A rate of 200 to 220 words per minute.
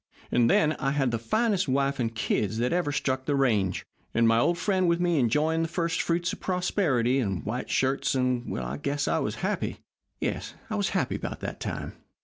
Yes: fast, 205 wpm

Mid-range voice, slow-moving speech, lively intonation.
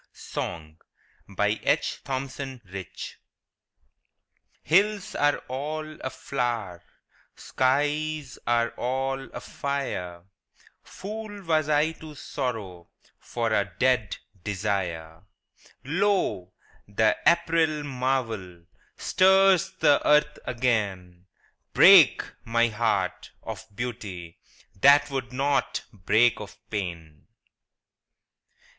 No: low, 125 Hz; slow, 85 wpm; wide, 6.6 semitones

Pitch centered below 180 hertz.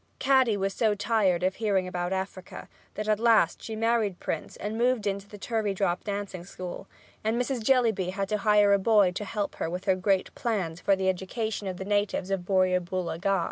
No: high, 200 Hz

